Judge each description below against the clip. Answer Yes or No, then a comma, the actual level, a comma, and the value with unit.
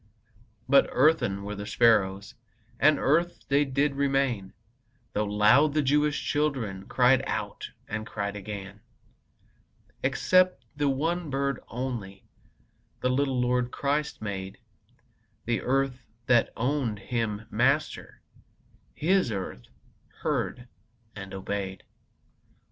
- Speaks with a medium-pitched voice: No, low, 125 Hz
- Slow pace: Yes, slow, 110 wpm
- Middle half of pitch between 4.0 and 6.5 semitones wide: Yes, wide, 5.4 semitones